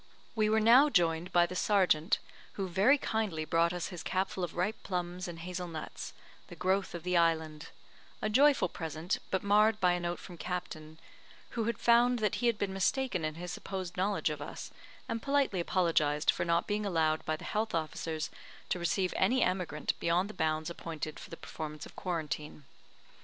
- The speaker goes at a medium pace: Yes, average, 190 wpm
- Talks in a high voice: No, medium, 180 Hz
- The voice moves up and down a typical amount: Yes, average, 4.0 semitones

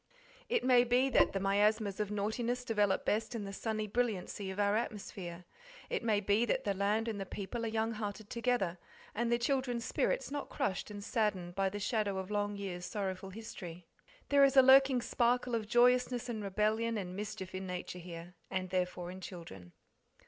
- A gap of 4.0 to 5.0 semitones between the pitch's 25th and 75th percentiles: No, average, 3.6 semitones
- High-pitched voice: Yes, high, 210 Hz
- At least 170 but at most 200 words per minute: Yes, average, 190 wpm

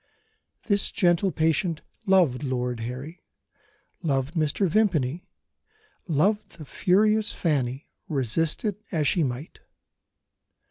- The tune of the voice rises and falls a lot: Yes, wide, 5.9 semitones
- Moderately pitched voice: Yes, medium, 160 Hz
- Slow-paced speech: Yes, slow, 100 wpm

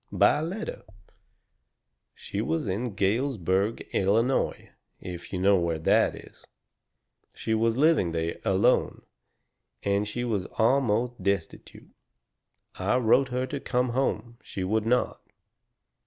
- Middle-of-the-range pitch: No, low, 110 Hz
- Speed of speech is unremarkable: No, slow, 120 wpm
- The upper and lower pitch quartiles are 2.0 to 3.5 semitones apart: No, average, 4.6 semitones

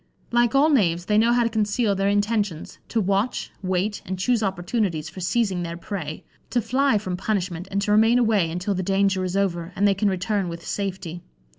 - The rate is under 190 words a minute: No, average, 200 wpm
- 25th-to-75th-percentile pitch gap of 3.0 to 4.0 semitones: Yes, average, 3.4 semitones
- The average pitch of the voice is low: No, high, 200 Hz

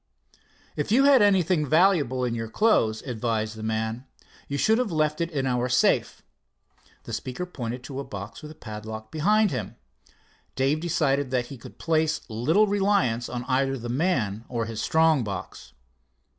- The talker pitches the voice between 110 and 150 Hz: Yes, low, 135 Hz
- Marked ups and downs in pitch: Yes, wide, 6.0 semitones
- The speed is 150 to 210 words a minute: Yes, average, 170 wpm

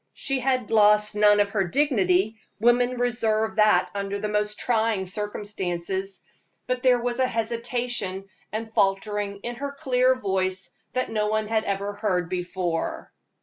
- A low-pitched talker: No, high, 210 Hz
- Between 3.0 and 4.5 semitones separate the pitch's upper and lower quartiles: Yes, average, 3.5 semitones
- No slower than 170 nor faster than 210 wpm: No, average, 145 wpm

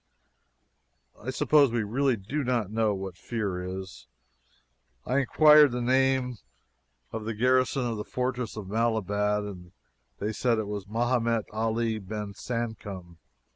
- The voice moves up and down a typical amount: Yes, average, 3.5 semitones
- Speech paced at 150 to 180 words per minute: No, slow, 135 wpm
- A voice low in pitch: Yes, low, 115 Hz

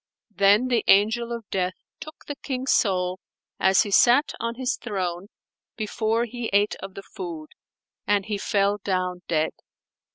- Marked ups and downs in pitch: No, average, 4.0 semitones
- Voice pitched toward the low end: No, high, 205 Hz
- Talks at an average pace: Yes, average, 155 wpm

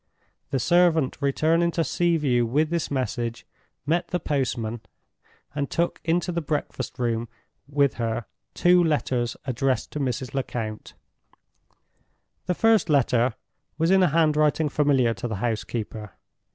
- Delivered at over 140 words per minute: No, slow, 135 wpm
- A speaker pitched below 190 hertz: Yes, medium, 140 Hz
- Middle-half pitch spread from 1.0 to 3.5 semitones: No, wide, 5.4 semitones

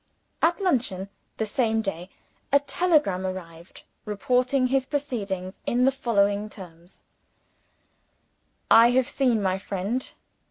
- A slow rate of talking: Yes, slow, 115 wpm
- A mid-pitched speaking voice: No, high, 220 Hz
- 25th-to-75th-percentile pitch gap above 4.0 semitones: Yes, wide, 5.4 semitones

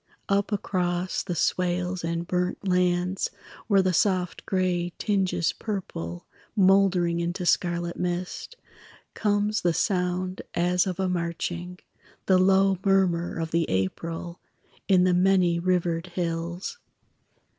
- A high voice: No, medium, 180 Hz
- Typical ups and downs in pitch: No, narrow, 1.7 semitones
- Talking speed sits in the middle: No, slow, 120 wpm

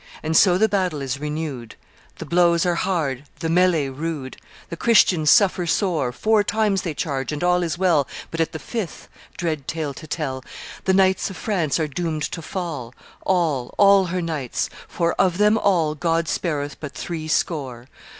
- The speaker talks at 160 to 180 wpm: Yes, average, 175 wpm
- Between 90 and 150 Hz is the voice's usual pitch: No, medium, 165 Hz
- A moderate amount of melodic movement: Yes, average, 3.7 semitones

